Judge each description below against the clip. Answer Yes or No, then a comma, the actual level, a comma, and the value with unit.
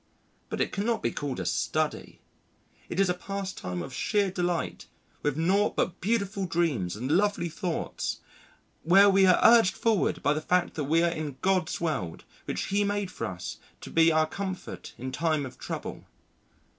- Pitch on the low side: No, medium, 175 Hz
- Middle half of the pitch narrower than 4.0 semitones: No, average, 4.7 semitones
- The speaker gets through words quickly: No, average, 175 wpm